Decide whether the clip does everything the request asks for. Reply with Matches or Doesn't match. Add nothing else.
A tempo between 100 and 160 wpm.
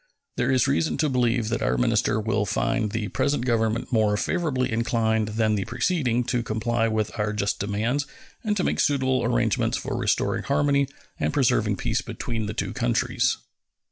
Doesn't match